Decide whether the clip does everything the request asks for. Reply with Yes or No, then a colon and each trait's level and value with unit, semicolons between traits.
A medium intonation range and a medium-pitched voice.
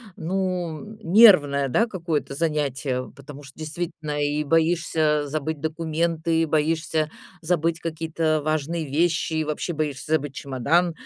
No: narrow, 2.2 semitones; medium, 155 Hz